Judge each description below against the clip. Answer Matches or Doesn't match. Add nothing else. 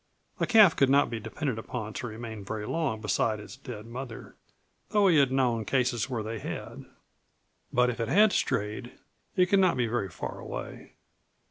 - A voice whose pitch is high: Doesn't match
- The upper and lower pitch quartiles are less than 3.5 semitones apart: Doesn't match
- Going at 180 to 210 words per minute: Matches